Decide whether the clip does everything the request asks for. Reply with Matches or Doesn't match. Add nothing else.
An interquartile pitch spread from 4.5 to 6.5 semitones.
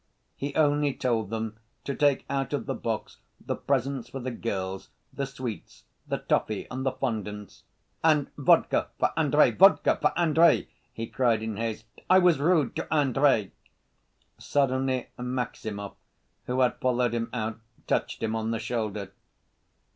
Doesn't match